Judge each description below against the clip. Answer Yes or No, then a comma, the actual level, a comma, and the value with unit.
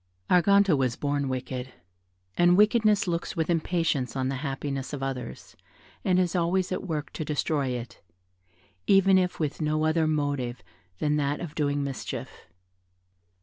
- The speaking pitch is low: No, medium, 150 Hz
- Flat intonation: No, average, 4.4 semitones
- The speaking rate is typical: Yes, average, 150 wpm